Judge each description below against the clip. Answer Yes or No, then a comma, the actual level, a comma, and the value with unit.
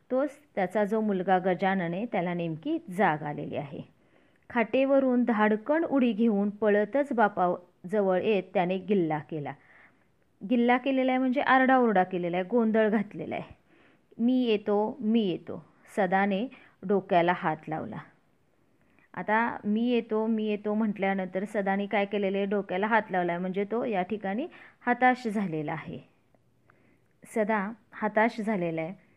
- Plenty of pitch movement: No, average, 3.8 semitones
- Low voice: No, high, 210 Hz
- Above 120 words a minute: Yes, fast, 130 wpm